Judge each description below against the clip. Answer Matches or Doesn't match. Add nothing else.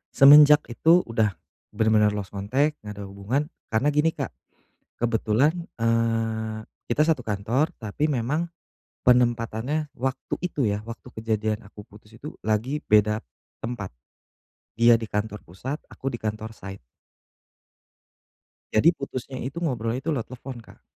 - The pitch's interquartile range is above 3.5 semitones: Matches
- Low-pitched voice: Matches